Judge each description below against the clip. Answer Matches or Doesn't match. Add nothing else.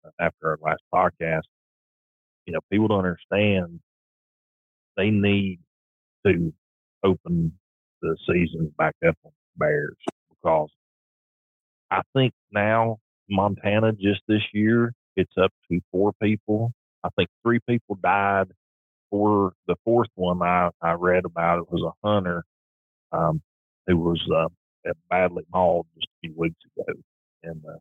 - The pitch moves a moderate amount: Matches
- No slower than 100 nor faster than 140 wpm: Matches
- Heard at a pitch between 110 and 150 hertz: Doesn't match